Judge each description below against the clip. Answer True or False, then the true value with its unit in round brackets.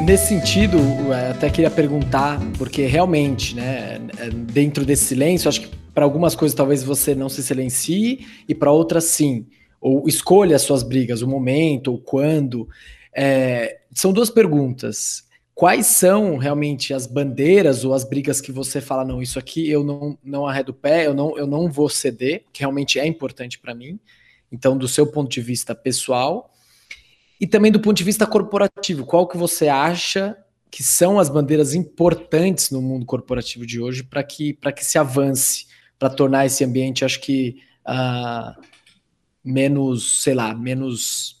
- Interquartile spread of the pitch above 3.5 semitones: False (3.2 semitones)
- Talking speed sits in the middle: True (165 wpm)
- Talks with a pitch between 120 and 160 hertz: True (140 Hz)